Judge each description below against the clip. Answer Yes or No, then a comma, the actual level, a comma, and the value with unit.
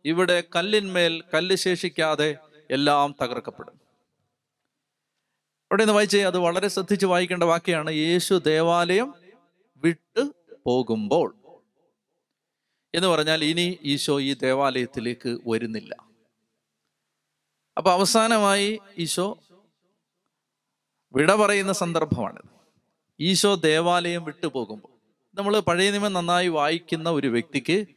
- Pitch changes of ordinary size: Yes, average, 4.1 semitones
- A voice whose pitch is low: No, medium, 175 Hz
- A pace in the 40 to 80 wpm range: No, average, 90 wpm